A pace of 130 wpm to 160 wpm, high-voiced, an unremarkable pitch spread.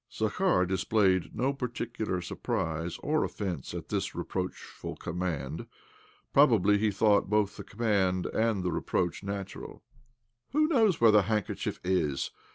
No: average, 140 wpm; low, 105 Hz; average, 4.2 semitones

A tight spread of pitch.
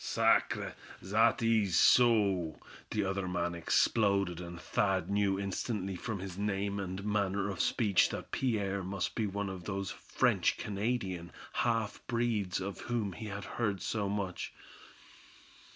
Yes: narrow, 2.1 semitones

